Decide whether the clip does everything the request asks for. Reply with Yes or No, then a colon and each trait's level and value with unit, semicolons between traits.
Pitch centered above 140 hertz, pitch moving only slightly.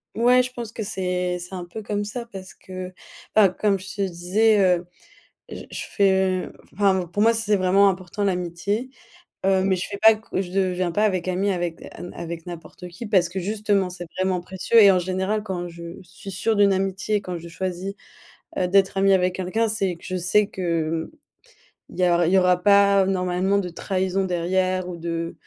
Yes: high, 190 Hz; narrow, 2.0 semitones